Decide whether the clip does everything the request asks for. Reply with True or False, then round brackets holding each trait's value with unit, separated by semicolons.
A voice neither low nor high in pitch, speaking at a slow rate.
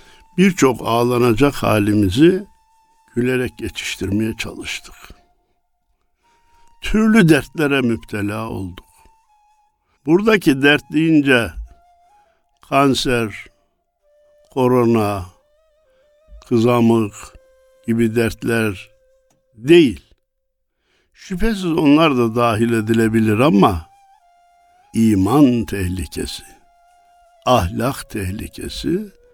True (145 Hz; 60 wpm)